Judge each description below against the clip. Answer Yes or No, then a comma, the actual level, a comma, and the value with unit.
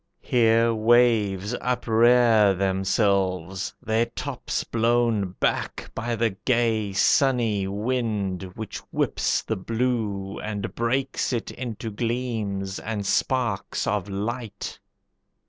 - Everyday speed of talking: No, slow, 100 wpm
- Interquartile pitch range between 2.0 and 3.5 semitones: Yes, average, 3.2 semitones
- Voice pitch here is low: Yes, low, 110 Hz